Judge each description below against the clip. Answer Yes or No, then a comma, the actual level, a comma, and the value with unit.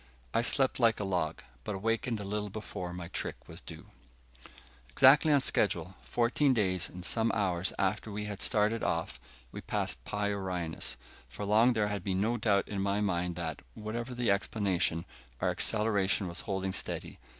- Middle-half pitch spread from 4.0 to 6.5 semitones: No, average, 3.3 semitones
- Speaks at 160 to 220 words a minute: Yes, average, 170 wpm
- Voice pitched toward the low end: Yes, low, 100 Hz